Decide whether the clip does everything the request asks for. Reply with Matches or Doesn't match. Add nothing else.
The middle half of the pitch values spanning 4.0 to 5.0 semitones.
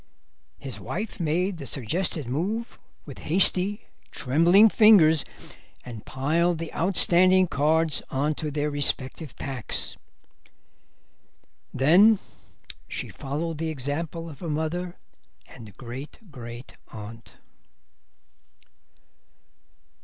Matches